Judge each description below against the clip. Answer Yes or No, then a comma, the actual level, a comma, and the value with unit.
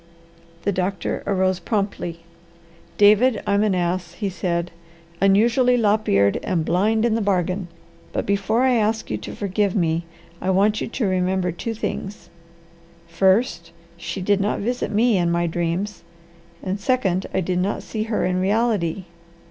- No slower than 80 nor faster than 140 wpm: No, average, 155 wpm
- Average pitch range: Yes, average, 3.1 semitones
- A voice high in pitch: Yes, high, 195 Hz